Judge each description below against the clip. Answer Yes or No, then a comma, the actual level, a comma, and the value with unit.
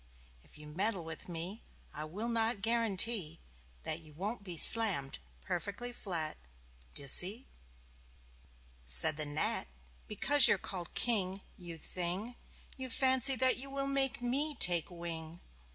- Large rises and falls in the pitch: Yes, wide, 6.5 semitones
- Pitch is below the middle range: No, high, 195 Hz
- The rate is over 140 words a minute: No, slow, 135 wpm